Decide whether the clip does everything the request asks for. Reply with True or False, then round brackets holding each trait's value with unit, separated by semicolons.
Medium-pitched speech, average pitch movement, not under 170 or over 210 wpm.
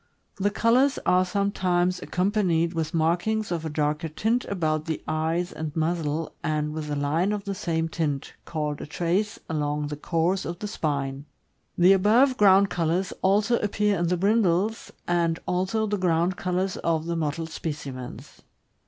False (170 Hz; 3.9 semitones; 160 wpm)